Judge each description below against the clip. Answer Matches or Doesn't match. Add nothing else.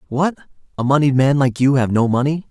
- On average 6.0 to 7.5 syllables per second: Doesn't match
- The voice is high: Doesn't match